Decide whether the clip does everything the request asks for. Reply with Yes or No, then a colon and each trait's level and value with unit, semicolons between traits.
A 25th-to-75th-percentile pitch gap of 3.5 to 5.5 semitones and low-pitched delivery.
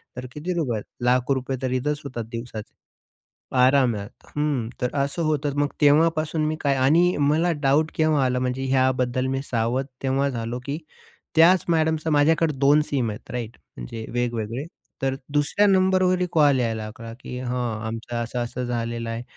Yes: average, 4.1 semitones; low, 130 Hz